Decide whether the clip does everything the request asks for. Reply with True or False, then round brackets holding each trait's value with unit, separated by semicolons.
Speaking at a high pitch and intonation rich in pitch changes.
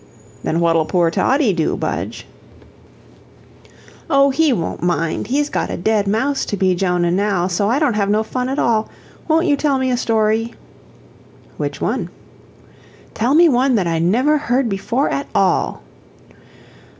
True (220 Hz; 6.6 semitones)